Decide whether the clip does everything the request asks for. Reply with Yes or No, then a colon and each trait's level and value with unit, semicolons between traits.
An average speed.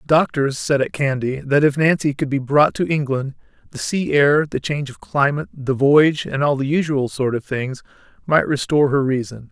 No: fast, 210 wpm